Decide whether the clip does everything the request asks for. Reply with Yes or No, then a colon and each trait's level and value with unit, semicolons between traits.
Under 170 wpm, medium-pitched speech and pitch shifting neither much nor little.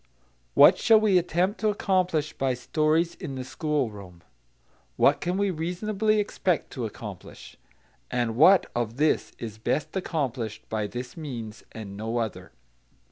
No: average, 140 wpm; medium, 145 Hz; wide, 8.1 semitones